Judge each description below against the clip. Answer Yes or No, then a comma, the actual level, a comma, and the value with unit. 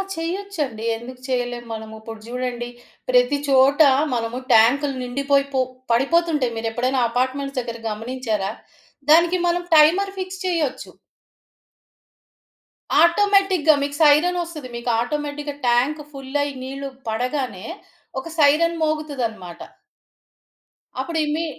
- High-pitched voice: Yes, very high, 275 Hz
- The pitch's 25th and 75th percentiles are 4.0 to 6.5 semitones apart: Yes, average, 4.4 semitones